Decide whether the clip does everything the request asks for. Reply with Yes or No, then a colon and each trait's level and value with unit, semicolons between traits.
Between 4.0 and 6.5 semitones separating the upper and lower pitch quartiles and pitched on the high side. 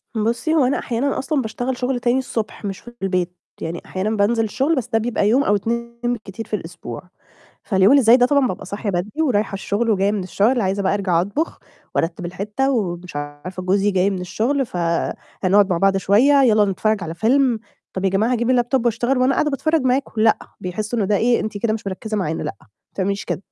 Yes: average, 4.3 semitones; high, 215 Hz